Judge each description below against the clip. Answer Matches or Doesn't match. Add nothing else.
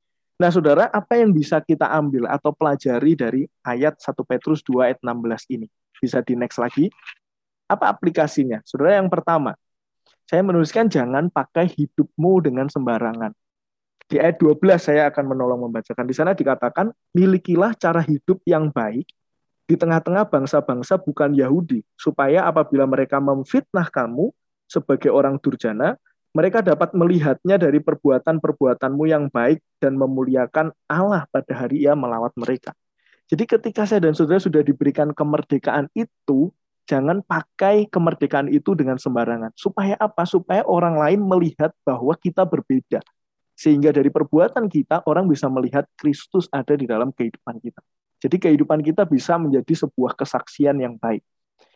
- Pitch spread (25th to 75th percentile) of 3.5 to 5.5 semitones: Matches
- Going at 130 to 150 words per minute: Matches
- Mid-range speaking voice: Matches